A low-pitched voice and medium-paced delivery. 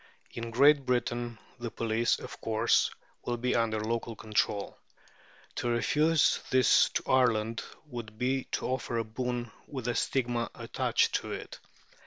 Yes: low, 120 Hz; average, 145 wpm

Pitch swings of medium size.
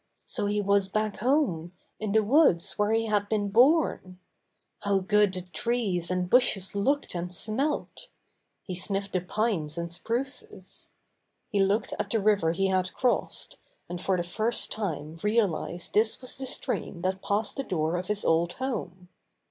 Yes: average, 3.5 semitones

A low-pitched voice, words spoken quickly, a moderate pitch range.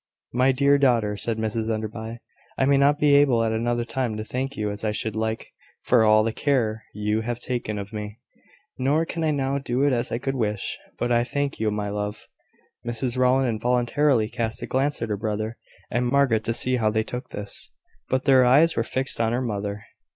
Yes: low, 120 Hz; fast, 210 wpm; average, 3.4 semitones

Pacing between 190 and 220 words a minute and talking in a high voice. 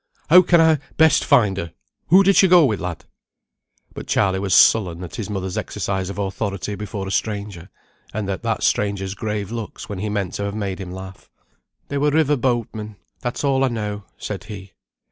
No: average, 195 wpm; low, 105 Hz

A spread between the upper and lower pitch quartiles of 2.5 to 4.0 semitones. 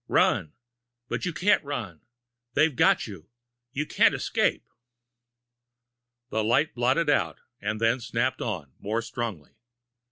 No: average, 4.7 semitones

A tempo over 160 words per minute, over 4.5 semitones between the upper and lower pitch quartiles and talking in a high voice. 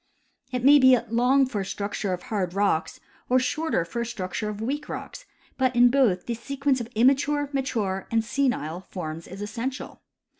Yes: average, 180 wpm; average, 5.2 semitones; high, 235 Hz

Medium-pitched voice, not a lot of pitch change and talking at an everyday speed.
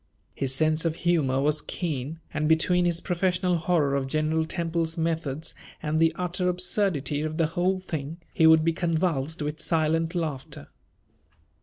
Yes: medium, 160 Hz; narrow, 2.2 semitones; average, 155 wpm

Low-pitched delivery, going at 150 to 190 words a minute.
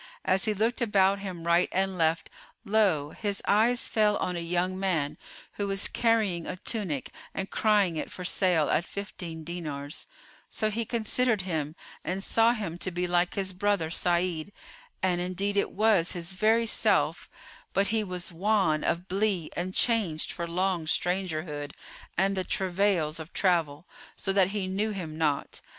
No: medium, 185 Hz; average, 165 wpm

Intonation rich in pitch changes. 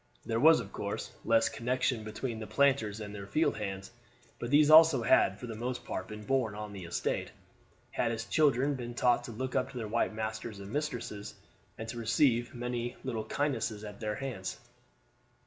No: average, 3.2 semitones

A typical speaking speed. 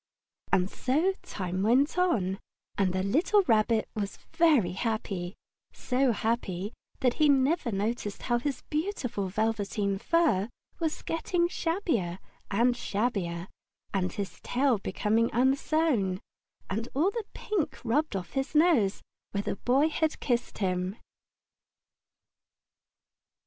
No: slow, 120 wpm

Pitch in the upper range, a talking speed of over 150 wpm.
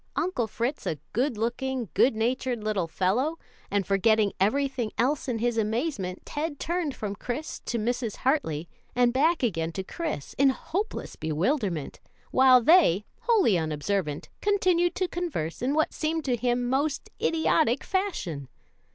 No: high, 245 Hz; average, 145 wpm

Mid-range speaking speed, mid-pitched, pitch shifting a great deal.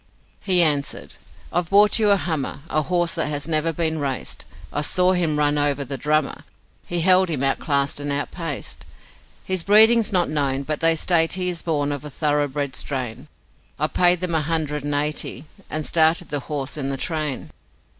No: average, 185 wpm; medium, 155 Hz; average, 3.2 semitones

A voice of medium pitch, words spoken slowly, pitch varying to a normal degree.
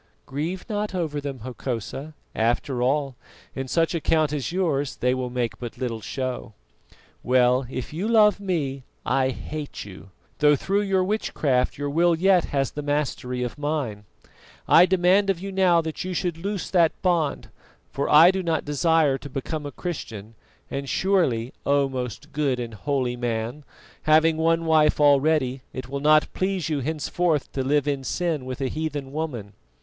No: medium, 145 Hz; average, 170 wpm; average, 4.4 semitones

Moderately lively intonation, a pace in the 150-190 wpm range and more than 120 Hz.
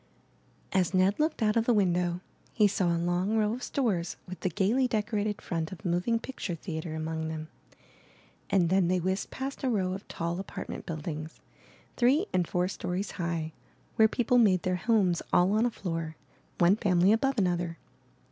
Yes: average, 4.0 semitones; average, 180 wpm; medium, 185 Hz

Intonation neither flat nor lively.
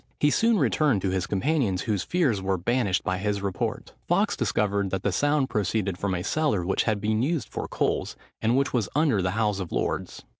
No: wide, 6.2 semitones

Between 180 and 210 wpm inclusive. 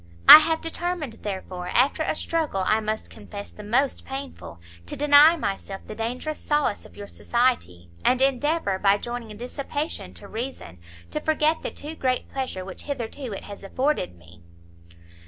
No: average, 160 wpm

